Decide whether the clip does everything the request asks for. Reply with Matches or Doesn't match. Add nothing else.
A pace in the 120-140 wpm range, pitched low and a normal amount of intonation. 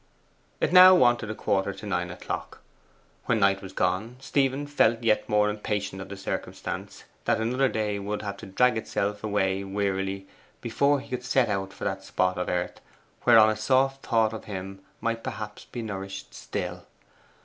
Doesn't match